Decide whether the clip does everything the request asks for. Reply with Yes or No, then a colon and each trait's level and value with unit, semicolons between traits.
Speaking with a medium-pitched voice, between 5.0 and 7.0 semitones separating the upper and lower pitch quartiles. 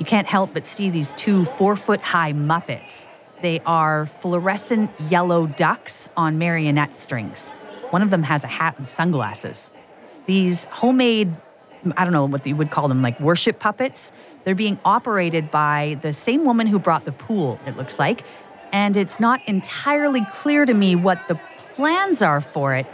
Yes: medium, 175 Hz; average, 5.3 semitones